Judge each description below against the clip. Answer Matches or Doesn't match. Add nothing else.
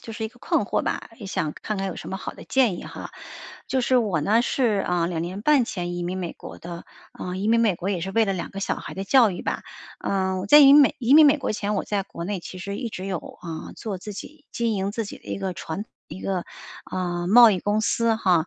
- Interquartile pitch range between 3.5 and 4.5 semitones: Matches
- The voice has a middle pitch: Doesn't match